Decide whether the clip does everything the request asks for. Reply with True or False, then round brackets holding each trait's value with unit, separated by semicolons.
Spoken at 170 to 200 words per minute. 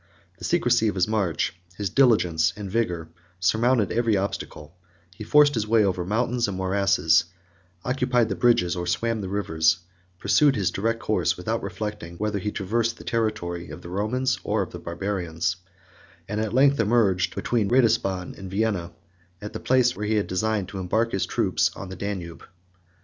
True (175 wpm)